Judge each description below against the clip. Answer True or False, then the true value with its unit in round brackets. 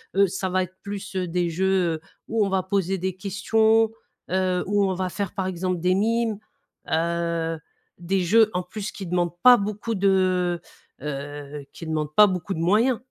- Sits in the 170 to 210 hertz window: True (185 Hz)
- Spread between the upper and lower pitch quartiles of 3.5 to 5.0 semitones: False (2.6 semitones)